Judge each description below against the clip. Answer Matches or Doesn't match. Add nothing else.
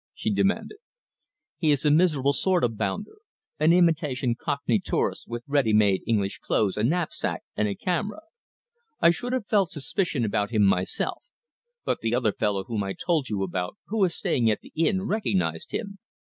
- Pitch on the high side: Doesn't match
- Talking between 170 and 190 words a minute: Matches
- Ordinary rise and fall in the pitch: Doesn't match